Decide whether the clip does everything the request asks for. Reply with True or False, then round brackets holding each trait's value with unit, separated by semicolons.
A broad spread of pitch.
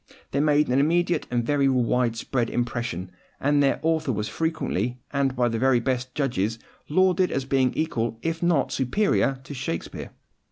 False (3.8 semitones)